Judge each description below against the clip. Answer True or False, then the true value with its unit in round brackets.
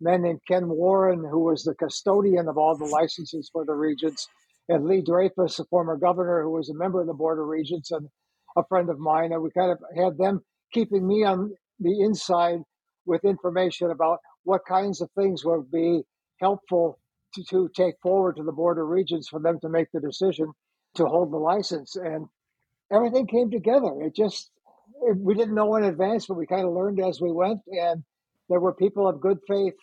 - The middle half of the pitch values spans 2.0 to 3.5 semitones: True (2.8 semitones)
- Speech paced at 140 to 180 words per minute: False (205 wpm)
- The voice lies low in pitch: False (180 Hz)